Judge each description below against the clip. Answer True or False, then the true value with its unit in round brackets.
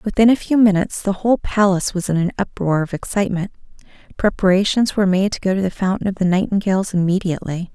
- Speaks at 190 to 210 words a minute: True (195 wpm)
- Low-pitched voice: False (190 Hz)